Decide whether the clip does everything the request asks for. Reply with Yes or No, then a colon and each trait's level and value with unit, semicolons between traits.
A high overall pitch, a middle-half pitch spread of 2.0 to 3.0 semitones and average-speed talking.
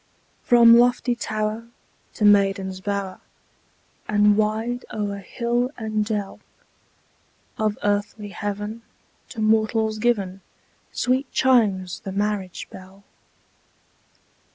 No: high, 210 Hz; narrow, 2.4 semitones; slow, 95 wpm